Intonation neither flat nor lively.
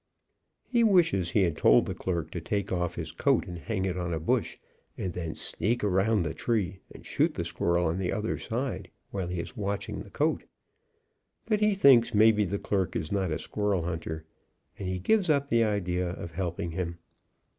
Yes: average, 4.2 semitones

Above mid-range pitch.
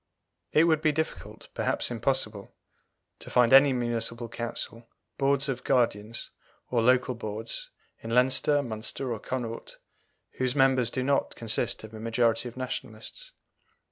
No: low, 125 Hz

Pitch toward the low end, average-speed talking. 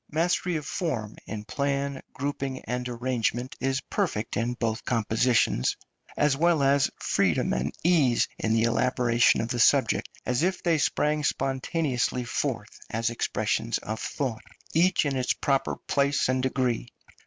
Yes: low, 130 Hz; average, 145 wpm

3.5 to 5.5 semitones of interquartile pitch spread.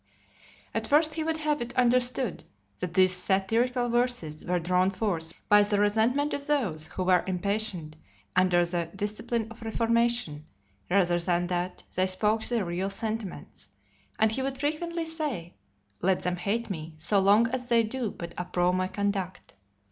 Yes: average, 5.0 semitones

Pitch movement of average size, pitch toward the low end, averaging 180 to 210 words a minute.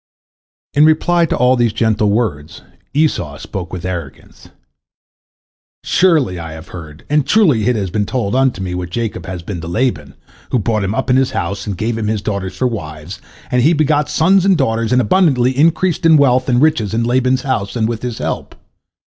No: wide, 6.0 semitones; low, 115 Hz; average, 200 wpm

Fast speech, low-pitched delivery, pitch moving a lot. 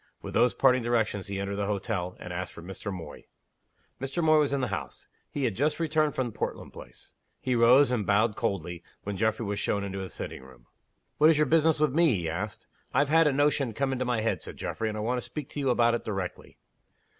Yes: fast, 235 wpm; low, 115 Hz; wide, 5.9 semitones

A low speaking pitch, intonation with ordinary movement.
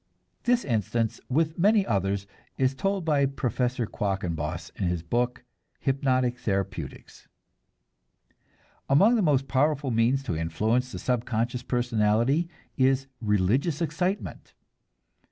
Yes: low, 125 Hz; average, 4.8 semitones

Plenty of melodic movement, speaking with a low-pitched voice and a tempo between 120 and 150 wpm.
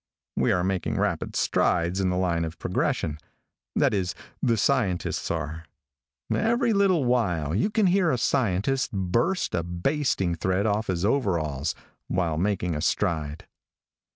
Yes: wide, 6.8 semitones; very low, 95 Hz; average, 145 wpm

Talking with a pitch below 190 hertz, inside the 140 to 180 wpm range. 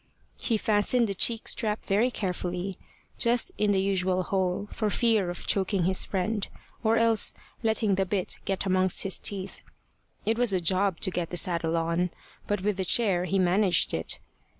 No: high, 195 Hz; average, 175 wpm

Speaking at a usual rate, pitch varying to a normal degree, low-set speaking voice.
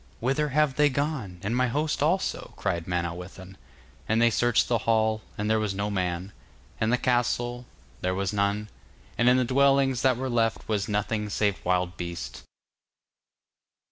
Yes: average, 170 wpm; average, 4.6 semitones; low, 110 Hz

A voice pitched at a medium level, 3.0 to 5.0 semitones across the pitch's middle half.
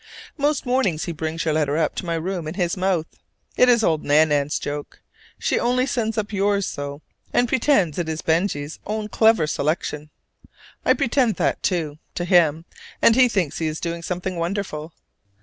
No: medium, 175 Hz; wide, 5.5 semitones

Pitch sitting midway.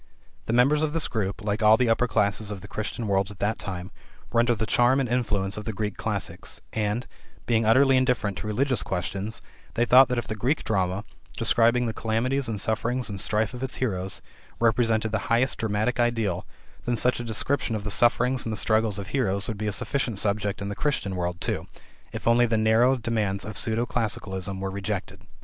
No: low, 110 Hz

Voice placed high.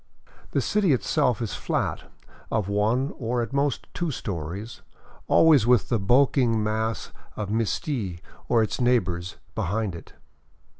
No: low, 115 Hz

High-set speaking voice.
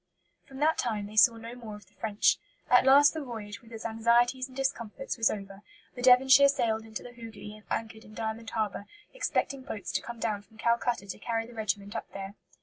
Yes: high, 230 Hz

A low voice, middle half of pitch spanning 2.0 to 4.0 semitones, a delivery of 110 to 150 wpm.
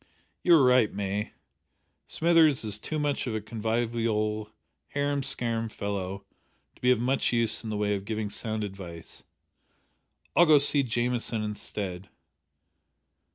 Yes: low, 110 Hz; average, 3.4 semitones; average, 145 wpm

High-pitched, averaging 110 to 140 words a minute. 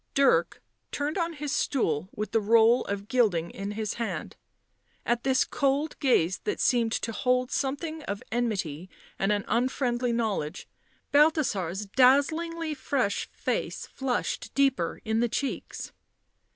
Yes: high, 240 Hz; slow, 135 wpm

